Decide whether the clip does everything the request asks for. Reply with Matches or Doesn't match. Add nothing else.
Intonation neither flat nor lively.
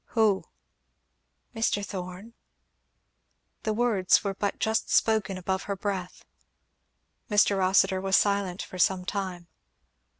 Doesn't match